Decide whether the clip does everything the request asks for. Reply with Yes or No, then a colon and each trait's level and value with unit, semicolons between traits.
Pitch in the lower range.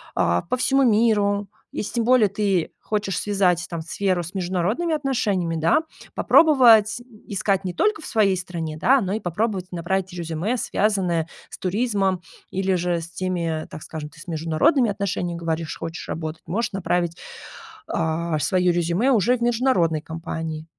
No: medium, 185 Hz